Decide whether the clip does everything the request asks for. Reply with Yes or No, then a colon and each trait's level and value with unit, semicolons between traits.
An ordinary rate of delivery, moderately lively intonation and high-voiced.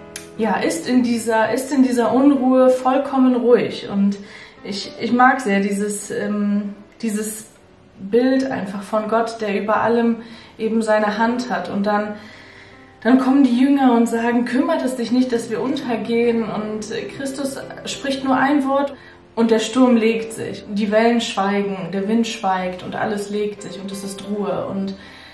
Yes: average, 170 wpm; average, 3.3 semitones; high, 225 Hz